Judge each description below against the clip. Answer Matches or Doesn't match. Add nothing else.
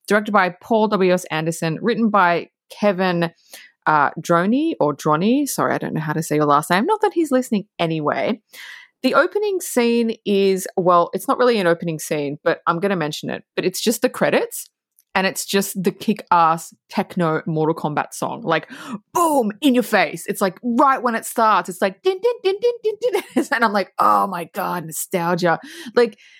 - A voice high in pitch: Matches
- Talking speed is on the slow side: Doesn't match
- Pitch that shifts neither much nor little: Doesn't match